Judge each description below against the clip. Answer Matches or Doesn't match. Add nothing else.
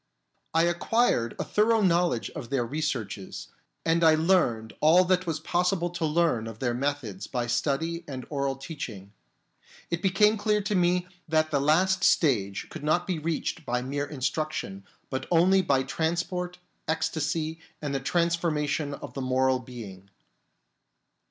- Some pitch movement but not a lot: Matches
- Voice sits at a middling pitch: Matches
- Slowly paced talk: Doesn't match